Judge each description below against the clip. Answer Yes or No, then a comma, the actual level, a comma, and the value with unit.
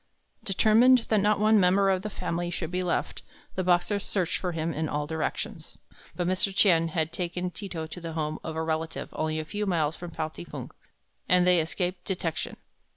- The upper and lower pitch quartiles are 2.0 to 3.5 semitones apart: Yes, average, 3.1 semitones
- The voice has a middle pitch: Yes, medium, 175 Hz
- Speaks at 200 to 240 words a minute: Yes, fast, 205 wpm